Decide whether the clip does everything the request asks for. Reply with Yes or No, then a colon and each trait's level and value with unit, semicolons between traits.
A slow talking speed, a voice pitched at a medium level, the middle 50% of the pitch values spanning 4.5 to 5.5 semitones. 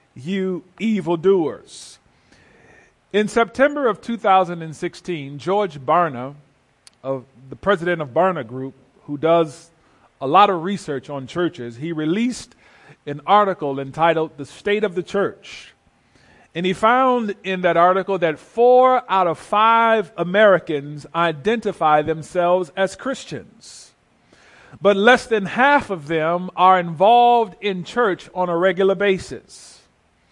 Yes: slow, 125 wpm; medium, 180 Hz; average, 4.8 semitones